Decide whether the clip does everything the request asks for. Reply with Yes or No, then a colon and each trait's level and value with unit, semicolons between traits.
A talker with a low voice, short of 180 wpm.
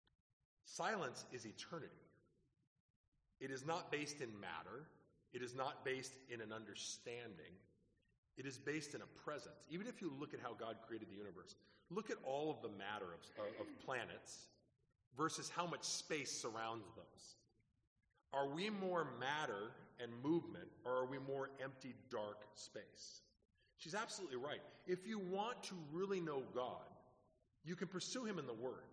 Yes: low, 130 Hz; average, 160 wpm